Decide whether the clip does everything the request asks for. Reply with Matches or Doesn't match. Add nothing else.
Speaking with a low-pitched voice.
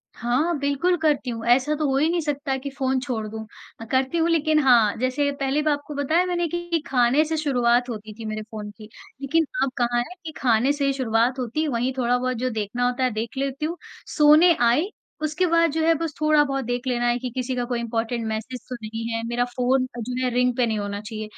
Doesn't match